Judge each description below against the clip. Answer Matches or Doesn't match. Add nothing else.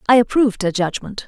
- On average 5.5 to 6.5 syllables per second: Matches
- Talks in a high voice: Matches